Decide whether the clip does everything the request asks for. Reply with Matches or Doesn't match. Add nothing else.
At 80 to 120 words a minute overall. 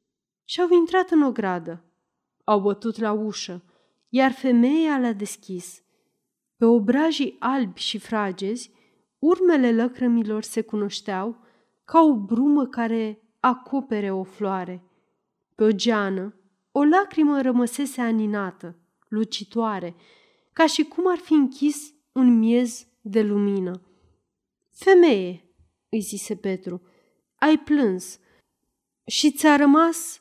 Matches